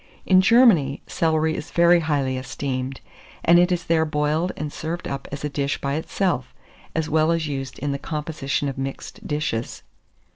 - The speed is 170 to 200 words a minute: Yes, average, 175 wpm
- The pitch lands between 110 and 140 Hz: No, medium, 150 Hz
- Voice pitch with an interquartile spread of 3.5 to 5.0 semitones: No, average, 3.1 semitones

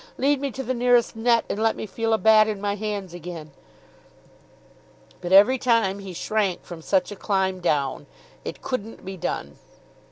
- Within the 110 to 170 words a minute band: No, average, 180 wpm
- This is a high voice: Yes, high, 210 Hz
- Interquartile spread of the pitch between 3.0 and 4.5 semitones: Yes, average, 3.4 semitones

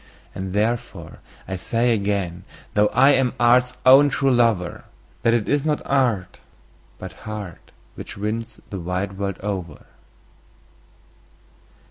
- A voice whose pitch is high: No, low, 105 Hz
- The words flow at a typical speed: No, slow, 125 wpm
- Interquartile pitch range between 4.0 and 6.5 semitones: Yes, average, 4.3 semitones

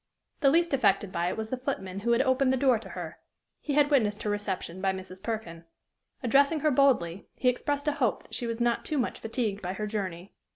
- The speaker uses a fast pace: Yes, fast, 225 wpm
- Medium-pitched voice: No, high, 225 Hz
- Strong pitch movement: Yes, wide, 6.0 semitones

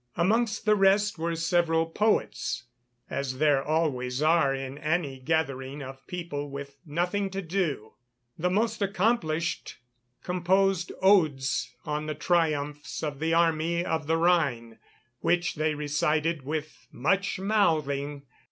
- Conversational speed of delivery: No, slow, 125 wpm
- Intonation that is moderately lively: Yes, average, 3.8 semitones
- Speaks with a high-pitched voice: No, medium, 160 Hz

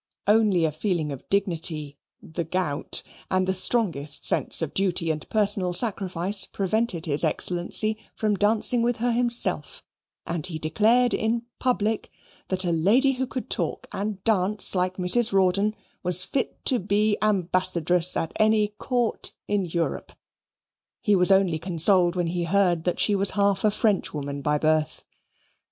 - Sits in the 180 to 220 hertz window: Yes, high, 190 Hz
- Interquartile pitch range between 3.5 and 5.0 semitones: Yes, average, 4.0 semitones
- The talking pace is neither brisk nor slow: Yes, average, 150 wpm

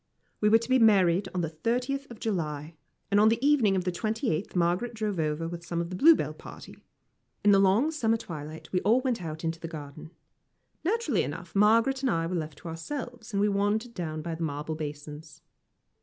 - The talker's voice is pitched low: No, high, 190 Hz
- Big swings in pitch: Yes, wide, 5.8 semitones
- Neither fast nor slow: No, fast, 210 wpm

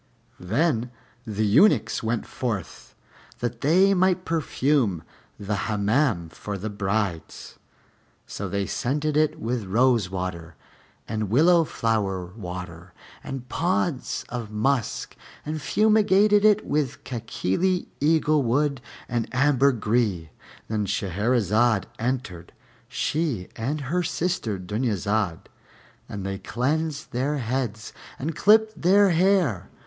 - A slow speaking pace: Yes, slow, 105 wpm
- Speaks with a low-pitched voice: Yes, low, 120 Hz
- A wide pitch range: Yes, wide, 7.1 semitones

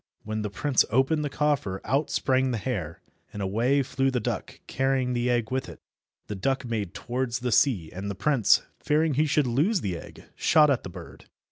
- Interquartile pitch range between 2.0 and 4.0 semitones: No, average, 4.6 semitones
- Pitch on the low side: Yes, low, 125 Hz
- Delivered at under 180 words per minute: No, fast, 205 wpm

